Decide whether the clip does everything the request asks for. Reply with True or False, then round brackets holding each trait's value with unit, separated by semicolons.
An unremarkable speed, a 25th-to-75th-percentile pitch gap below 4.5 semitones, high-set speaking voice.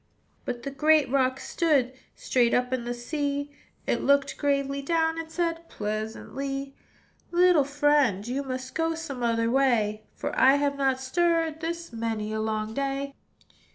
True (155 wpm; 3.9 semitones; 275 Hz)